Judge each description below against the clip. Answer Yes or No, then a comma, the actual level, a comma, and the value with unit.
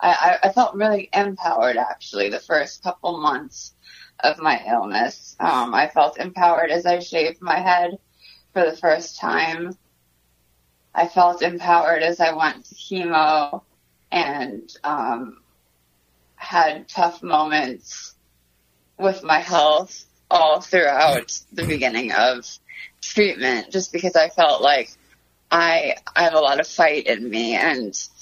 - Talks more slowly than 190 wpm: Yes, slow, 135 wpm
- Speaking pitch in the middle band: Yes, medium, 165 Hz